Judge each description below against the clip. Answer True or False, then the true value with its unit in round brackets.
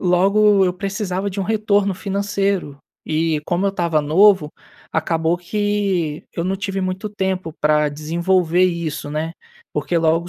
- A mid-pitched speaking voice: True (180 Hz)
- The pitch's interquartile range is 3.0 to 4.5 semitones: True (3.5 semitones)